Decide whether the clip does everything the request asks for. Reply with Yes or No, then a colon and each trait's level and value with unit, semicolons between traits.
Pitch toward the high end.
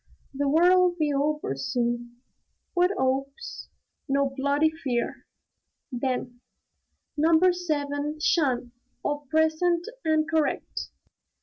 Yes: very high, 290 Hz